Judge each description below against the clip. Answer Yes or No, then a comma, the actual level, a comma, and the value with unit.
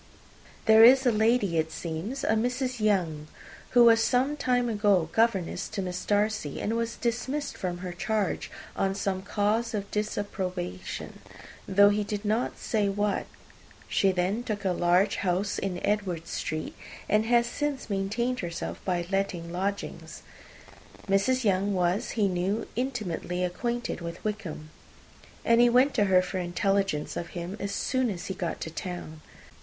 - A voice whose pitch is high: Yes, high, 200 Hz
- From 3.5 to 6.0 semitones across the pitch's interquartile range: Yes, average, 4.1 semitones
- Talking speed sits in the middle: Yes, average, 160 wpm